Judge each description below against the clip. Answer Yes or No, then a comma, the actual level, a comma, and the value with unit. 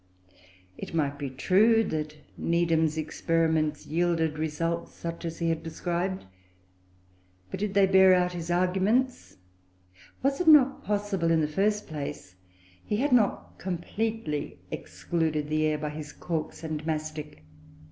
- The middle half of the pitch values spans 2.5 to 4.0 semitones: Yes, average, 3.7 semitones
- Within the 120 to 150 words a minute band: Yes, slow, 135 wpm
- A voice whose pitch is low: No, medium, 165 Hz